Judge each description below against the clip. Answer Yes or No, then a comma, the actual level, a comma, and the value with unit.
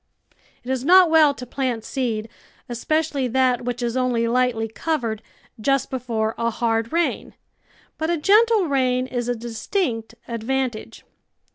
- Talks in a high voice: Yes, very high, 250 Hz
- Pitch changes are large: No, average, 3.3 semitones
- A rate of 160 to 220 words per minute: No, average, 140 wpm